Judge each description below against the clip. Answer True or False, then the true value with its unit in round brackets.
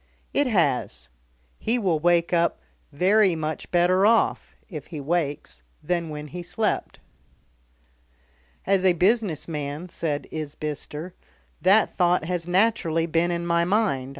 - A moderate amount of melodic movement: True (3.3 semitones)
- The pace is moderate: False (130 wpm)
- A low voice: False (175 Hz)